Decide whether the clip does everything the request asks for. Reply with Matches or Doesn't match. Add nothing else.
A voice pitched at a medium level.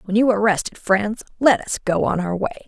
Doesn't match